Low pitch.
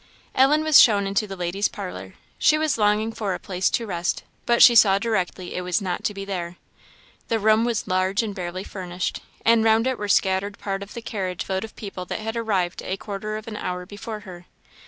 No: high, 200 Hz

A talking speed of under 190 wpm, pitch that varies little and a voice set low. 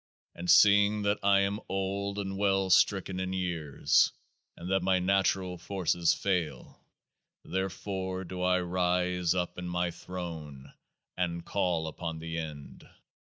Yes: average, 140 wpm; narrow, 2.0 semitones; very low, 90 Hz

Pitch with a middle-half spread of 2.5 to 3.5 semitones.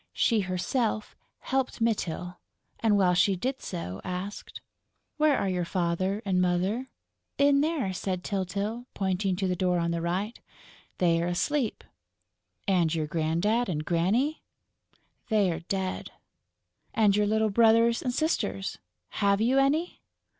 No: average, 4.4 semitones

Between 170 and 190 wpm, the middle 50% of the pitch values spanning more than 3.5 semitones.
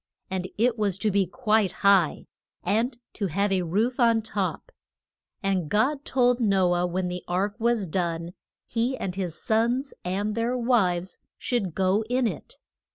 No: average, 160 wpm; average, 4.3 semitones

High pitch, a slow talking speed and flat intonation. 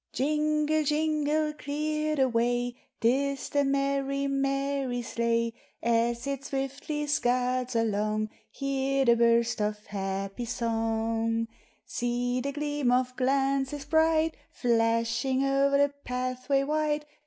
No: very high, 265 Hz; slow, 115 wpm; average, 3.3 semitones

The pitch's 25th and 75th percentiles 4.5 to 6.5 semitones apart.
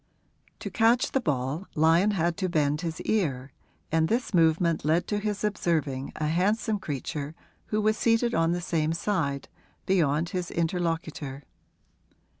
Yes: average, 4.8 semitones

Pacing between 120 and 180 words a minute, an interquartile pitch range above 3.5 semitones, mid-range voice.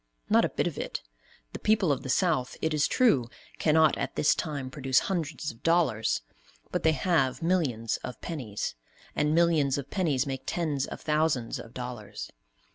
Yes: average, 175 wpm; average, 4.2 semitones; medium, 150 Hz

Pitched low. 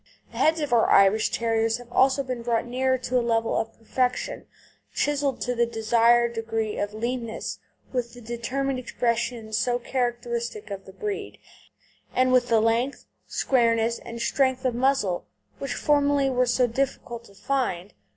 No: high, 240 Hz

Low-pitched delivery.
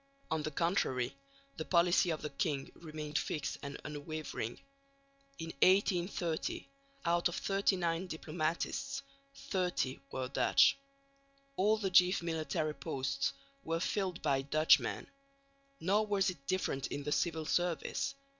No: medium, 165 Hz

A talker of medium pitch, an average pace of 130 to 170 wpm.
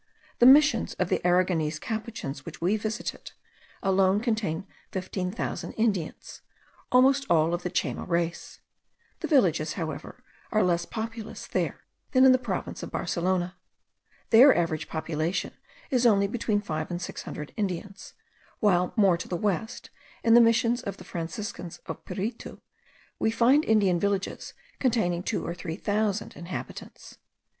No: high, 195 Hz; average, 145 wpm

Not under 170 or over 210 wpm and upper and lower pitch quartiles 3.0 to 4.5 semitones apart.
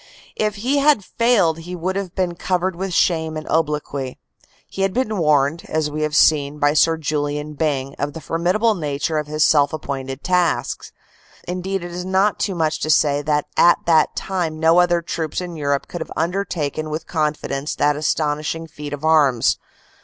Yes: average, 185 wpm; average, 3.3 semitones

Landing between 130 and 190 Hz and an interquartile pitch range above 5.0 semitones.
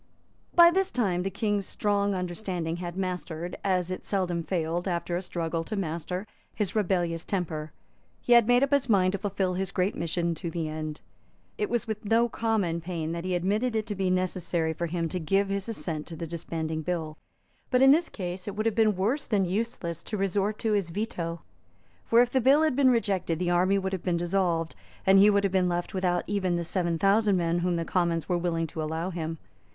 No: medium, 185 Hz; average, 3.3 semitones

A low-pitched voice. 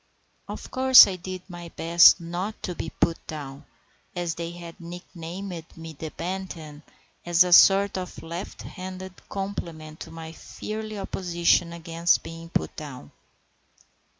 No: medium, 170 Hz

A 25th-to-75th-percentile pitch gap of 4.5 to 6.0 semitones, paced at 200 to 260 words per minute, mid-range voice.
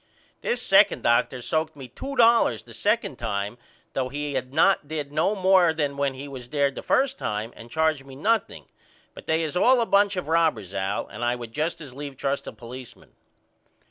Yes: average, 4.8 semitones; fast, 205 wpm; medium, 145 Hz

